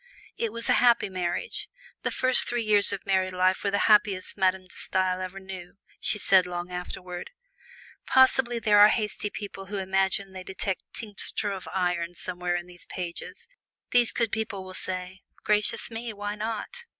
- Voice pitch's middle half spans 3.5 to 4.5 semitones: No, narrow, 2.5 semitones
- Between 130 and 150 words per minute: No, average, 175 wpm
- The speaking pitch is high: Yes, high, 195 Hz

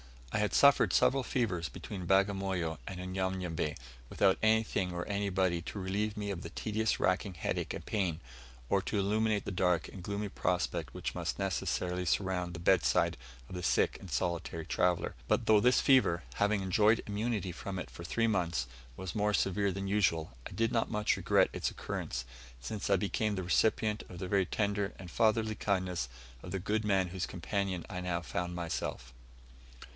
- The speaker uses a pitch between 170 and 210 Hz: No, very low, 95 Hz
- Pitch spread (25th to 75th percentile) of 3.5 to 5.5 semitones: No, average, 2.9 semitones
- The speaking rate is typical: Yes, average, 180 wpm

